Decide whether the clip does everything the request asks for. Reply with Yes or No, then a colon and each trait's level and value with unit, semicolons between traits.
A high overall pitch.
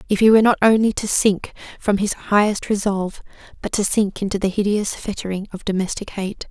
Yes: high, 200 Hz